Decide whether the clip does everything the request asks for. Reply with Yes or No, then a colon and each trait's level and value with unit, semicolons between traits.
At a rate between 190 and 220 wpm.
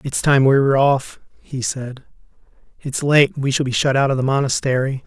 Yes: average, 200 wpm